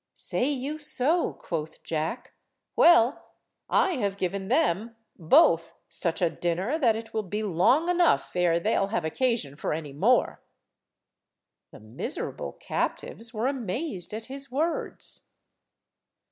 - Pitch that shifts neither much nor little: No, wide, 7.5 semitones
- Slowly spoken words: Yes, slow, 130 wpm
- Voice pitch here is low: No, high, 220 Hz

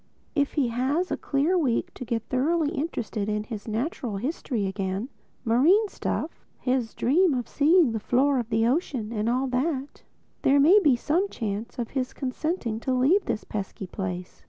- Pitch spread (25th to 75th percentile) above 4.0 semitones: Yes, average, 4.9 semitones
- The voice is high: Yes, very high, 255 Hz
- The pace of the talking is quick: No, average, 165 wpm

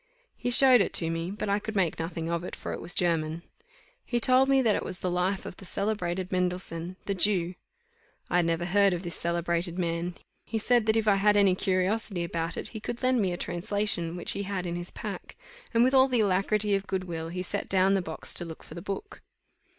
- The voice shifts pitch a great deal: No, average, 3.4 semitones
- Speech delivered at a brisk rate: Yes, fast, 235 wpm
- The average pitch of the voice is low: No, medium, 185 Hz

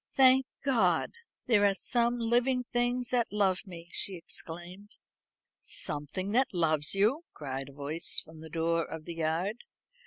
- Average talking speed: Yes, average, 150 wpm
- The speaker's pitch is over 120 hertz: Yes, high, 190 Hz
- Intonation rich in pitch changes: Yes, wide, 6.8 semitones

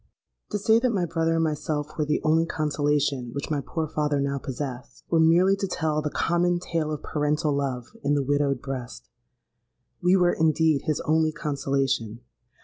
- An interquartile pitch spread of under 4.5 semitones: Yes, average, 2.7 semitones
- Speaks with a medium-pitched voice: Yes, medium, 150 Hz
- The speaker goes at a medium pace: Yes, average, 175 wpm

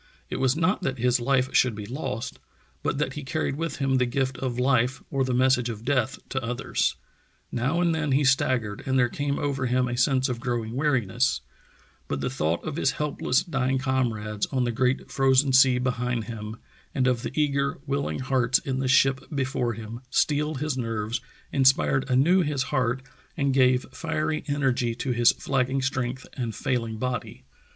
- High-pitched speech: No, low, 130 Hz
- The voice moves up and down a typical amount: No, narrow, 2.1 semitones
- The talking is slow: No, average, 190 wpm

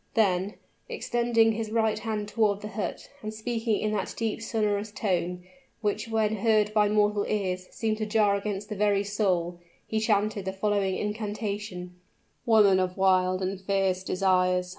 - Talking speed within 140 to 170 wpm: Yes, average, 160 wpm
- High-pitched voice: Yes, high, 205 Hz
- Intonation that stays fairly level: Yes, narrow, 2.2 semitones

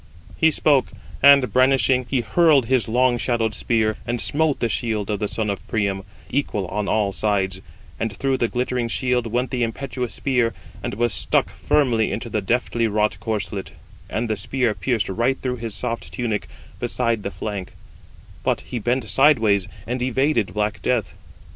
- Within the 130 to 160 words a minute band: No, average, 170 wpm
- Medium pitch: No, low, 115 Hz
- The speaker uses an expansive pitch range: No, average, 3.2 semitones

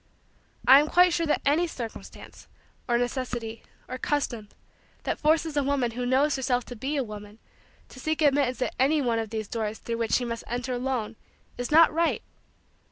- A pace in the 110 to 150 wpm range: No, average, 185 wpm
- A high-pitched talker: Yes, very high, 255 Hz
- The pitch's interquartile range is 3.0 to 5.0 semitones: Yes, average, 4.0 semitones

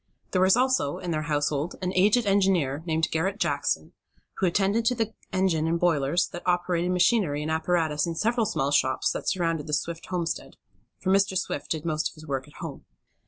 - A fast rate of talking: No, average, 195 wpm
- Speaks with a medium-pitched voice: Yes, medium, 170 Hz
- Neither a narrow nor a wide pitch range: Yes, average, 3.8 semitones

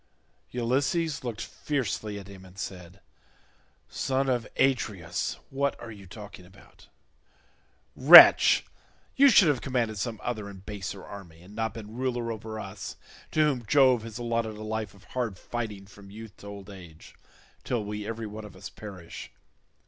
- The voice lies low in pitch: Yes, low, 110 Hz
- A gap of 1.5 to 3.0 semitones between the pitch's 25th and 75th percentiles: No, average, 3.5 semitones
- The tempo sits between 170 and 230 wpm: No, average, 160 wpm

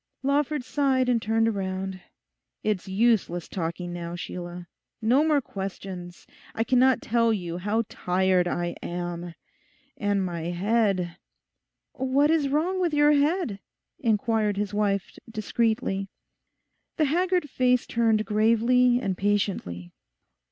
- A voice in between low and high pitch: No, high, 215 Hz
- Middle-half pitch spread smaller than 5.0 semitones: No, wide, 5.4 semitones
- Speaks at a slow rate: Yes, slow, 120 wpm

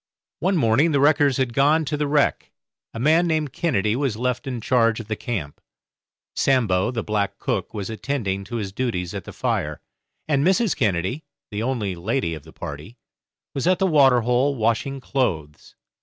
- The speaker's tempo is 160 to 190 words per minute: Yes, average, 180 wpm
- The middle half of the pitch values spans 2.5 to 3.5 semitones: No, average, 5.3 semitones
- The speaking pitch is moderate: No, low, 125 Hz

